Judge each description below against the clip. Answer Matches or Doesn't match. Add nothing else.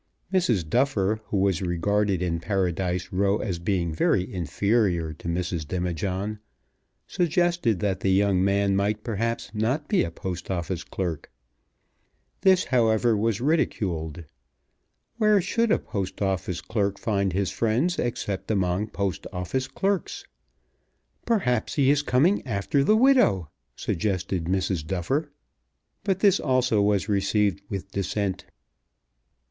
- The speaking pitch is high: Doesn't match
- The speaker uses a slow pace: Matches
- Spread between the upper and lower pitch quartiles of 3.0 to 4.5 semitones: Doesn't match